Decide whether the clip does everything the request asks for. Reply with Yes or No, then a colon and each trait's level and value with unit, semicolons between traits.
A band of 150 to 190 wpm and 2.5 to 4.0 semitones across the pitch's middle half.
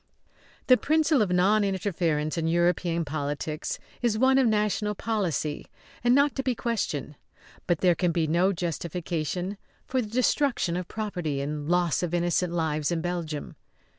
No: average, 155 wpm; average, 4.8 semitones